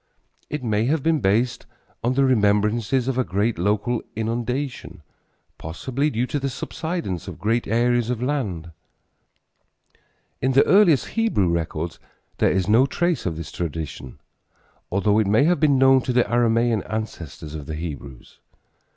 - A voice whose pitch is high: No, low, 115 Hz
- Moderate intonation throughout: No, wide, 5.7 semitones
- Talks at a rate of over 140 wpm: Yes, average, 150 wpm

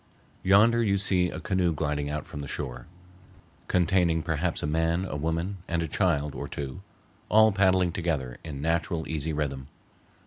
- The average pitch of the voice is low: Yes, very low, 80 Hz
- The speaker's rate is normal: Yes, average, 165 wpm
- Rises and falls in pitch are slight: No, average, 3.9 semitones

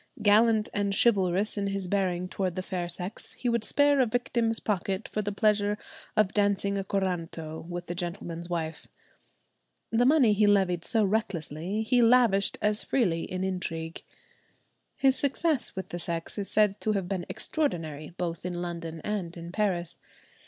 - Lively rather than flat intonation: No, average, 3.6 semitones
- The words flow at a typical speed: Yes, average, 165 wpm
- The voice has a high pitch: Yes, high, 195 Hz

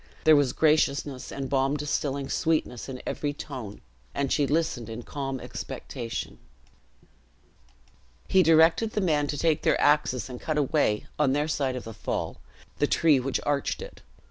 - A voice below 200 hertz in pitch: Yes, medium, 140 Hz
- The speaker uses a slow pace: No, average, 160 wpm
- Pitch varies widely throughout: No, average, 2.7 semitones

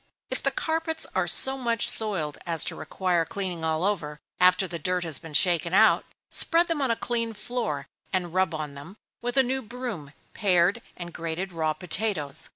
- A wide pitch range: Yes, wide, 6.1 semitones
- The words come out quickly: No, average, 185 wpm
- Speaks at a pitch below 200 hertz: Yes, medium, 185 Hz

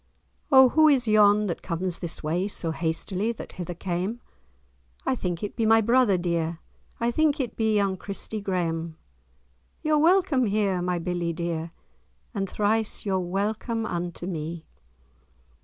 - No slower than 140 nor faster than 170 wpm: Yes, average, 150 wpm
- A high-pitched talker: Yes, high, 195 Hz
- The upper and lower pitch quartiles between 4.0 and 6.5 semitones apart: Yes, average, 4.5 semitones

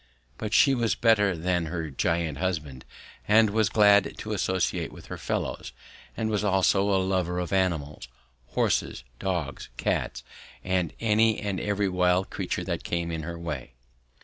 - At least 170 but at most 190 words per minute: No, average, 155 wpm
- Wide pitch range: No, average, 3.5 semitones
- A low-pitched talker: Yes, very low, 95 Hz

